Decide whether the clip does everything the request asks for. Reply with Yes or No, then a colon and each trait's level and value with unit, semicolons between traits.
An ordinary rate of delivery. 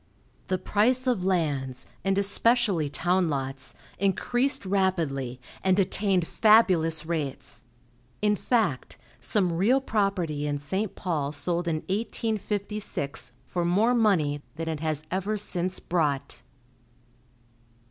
No: slow, 115 wpm